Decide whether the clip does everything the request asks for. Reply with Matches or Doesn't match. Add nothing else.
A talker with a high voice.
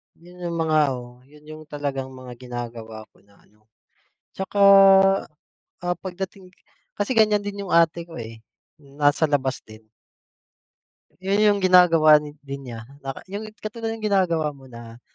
Doesn't match